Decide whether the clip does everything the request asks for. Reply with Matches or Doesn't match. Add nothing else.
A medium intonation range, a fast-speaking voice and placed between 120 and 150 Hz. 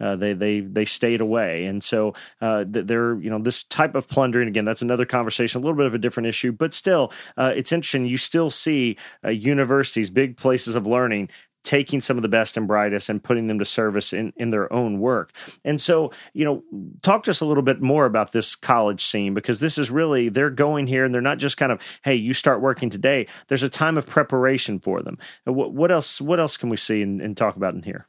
Matches